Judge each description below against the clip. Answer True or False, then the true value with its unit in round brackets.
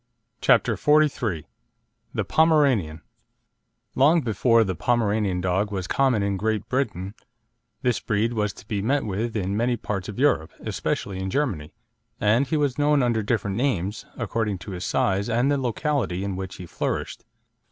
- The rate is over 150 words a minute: True (160 wpm)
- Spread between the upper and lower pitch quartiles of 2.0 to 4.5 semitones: False (5.0 semitones)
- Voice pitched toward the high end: False (110 Hz)